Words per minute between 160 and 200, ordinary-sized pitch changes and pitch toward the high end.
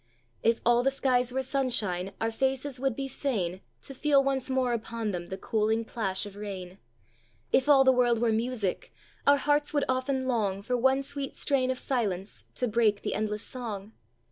Yes: average, 185 wpm; average, 4.0 semitones; high, 245 Hz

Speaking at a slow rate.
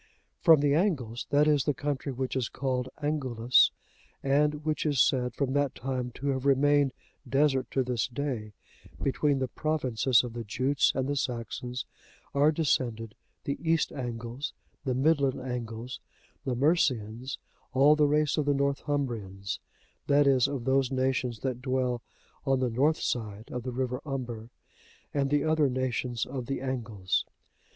No: average, 155 wpm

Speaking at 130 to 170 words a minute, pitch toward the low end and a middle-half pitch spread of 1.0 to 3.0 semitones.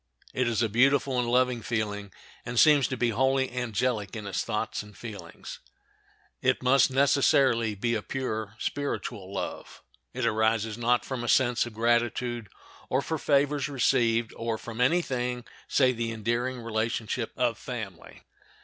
Yes: average, 155 wpm; low, 120 Hz; narrow, 2.4 semitones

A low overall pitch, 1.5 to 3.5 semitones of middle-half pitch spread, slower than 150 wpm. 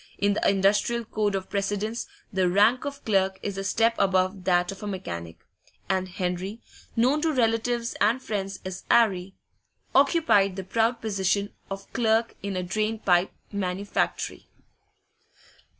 No: high, 200 Hz; average, 3.1 semitones; average, 140 wpm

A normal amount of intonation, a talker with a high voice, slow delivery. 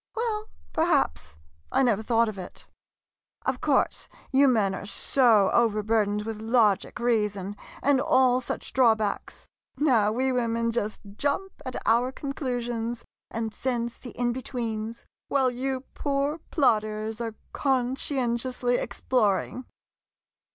Yes: average, 3.1 semitones; high, 240 Hz; slow, 130 wpm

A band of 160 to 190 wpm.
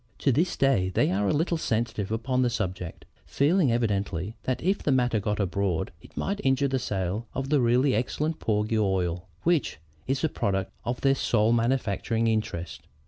Yes: average, 180 wpm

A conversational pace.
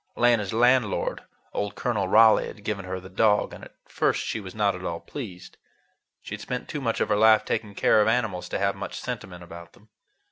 No: fast, 215 wpm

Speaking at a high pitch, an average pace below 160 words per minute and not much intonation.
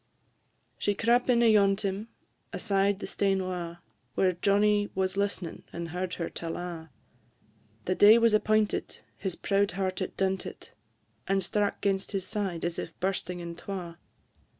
Yes: high, 195 Hz; average, 150 wpm; narrow, 2.2 semitones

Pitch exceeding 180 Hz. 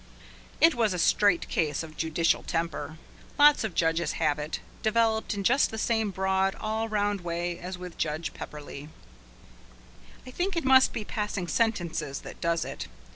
Yes: high, 190 Hz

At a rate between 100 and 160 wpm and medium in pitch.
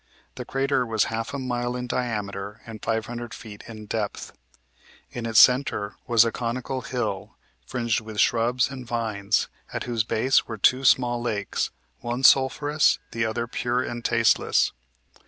No: average, 155 wpm; low, 120 Hz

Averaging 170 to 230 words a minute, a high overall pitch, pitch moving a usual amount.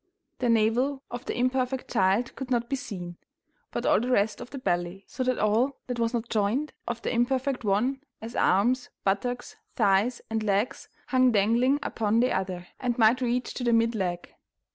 Yes: average, 185 wpm; high, 235 Hz; average, 3.5 semitones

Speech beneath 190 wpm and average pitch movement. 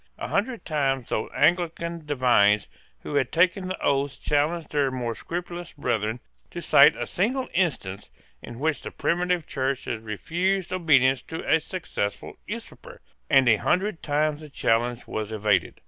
No: average, 155 wpm; wide, 6.1 semitones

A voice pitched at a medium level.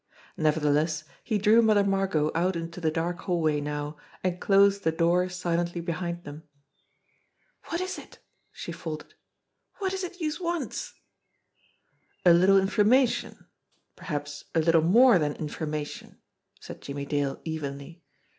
Yes: medium, 170 Hz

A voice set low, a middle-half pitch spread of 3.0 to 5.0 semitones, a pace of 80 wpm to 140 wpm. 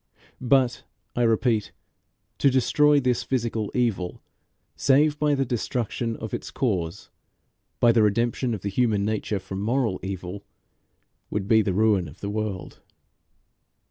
Yes: low, 110 Hz; average, 3.8 semitones; slow, 135 wpm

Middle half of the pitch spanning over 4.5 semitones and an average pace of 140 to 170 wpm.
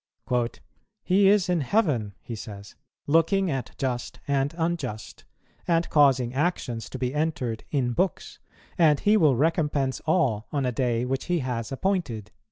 Yes: wide, 5.4 semitones; average, 150 wpm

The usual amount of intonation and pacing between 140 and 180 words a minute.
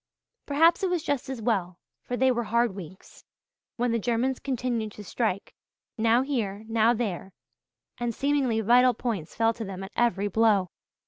Yes: average, 3.3 semitones; average, 170 wpm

